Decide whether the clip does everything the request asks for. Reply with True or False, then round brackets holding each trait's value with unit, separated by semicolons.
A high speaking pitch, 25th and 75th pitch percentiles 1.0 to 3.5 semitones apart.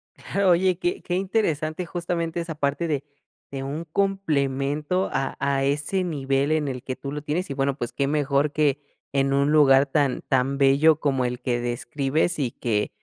False (145 Hz; 3.2 semitones)